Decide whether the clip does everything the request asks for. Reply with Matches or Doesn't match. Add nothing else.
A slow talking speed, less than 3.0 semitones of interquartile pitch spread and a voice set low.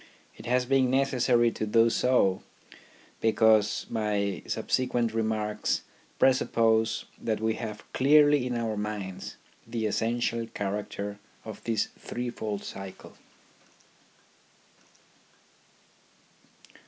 Matches